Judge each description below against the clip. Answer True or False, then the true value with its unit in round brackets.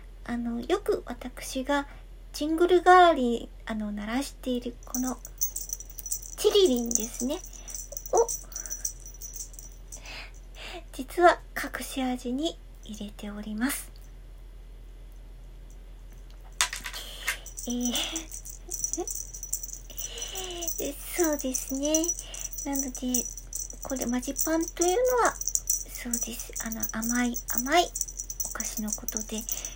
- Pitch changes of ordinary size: False (5.8 semitones)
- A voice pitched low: False (265 Hz)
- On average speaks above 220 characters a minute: False (170 characters per minute)